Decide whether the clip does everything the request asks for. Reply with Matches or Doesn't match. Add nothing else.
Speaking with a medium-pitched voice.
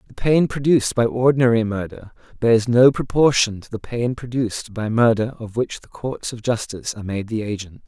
Doesn't match